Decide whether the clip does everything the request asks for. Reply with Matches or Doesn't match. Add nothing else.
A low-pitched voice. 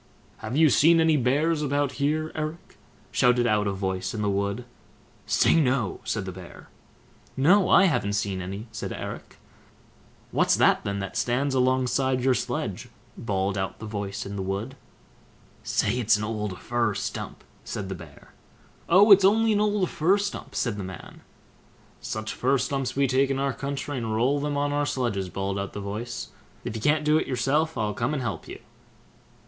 Matches